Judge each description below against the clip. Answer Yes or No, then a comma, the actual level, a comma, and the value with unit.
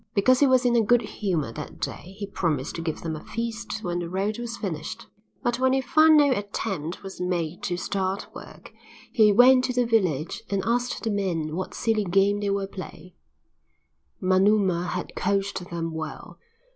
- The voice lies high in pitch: Yes, high, 195 Hz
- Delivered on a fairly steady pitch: No, average, 4.7 semitones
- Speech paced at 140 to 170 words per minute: No, average, 190 wpm